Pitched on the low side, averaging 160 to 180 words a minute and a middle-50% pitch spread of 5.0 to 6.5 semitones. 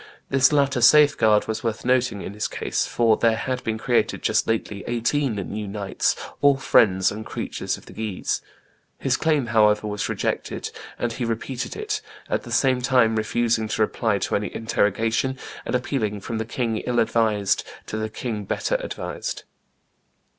No: low, 115 Hz; average, 170 wpm; average, 3.1 semitones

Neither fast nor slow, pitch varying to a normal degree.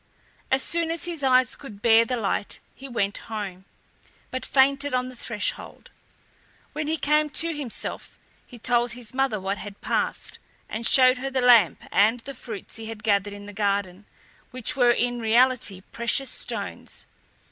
Yes: average, 170 wpm; average, 4.1 semitones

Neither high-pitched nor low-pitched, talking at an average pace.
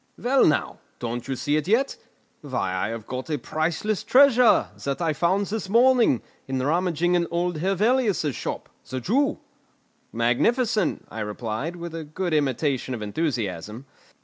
Yes: medium, 160 Hz; average, 150 wpm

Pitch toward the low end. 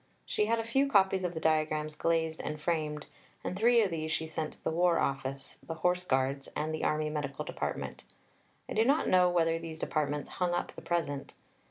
No: medium, 160 Hz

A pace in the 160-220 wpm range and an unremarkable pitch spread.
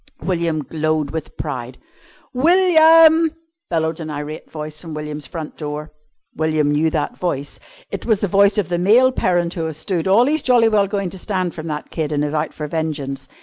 Yes: average, 190 wpm; average, 4.8 semitones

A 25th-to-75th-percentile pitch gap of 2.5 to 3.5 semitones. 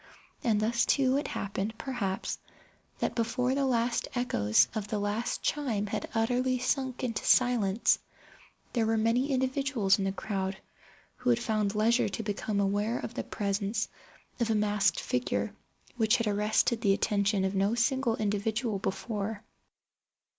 Yes: average, 3.2 semitones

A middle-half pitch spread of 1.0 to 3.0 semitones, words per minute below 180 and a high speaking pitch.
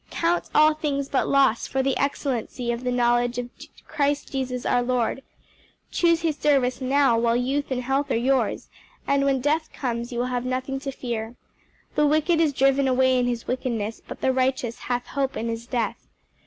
No: narrow, 2.4 semitones; average, 190 wpm; very high, 260 Hz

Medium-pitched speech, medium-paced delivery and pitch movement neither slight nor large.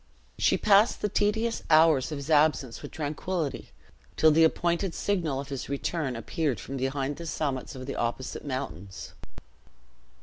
Yes: medium, 150 Hz; average, 155 wpm; average, 4.0 semitones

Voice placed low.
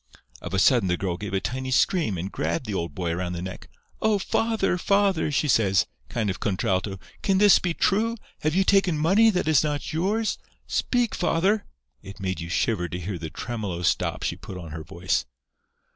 Yes: low, 115 Hz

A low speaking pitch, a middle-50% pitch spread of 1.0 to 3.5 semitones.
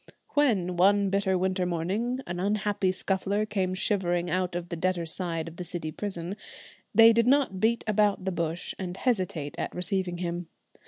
No: medium, 185 Hz; average, 2.7 semitones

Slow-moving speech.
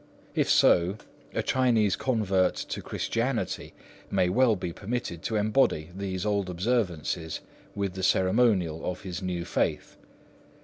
Yes: slow, 130 wpm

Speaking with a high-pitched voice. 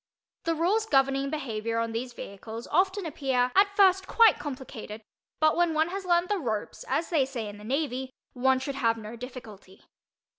Yes: very high, 270 Hz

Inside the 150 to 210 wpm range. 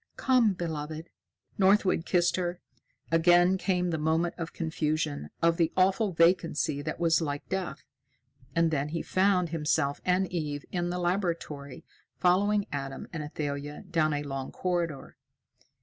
No: average, 140 wpm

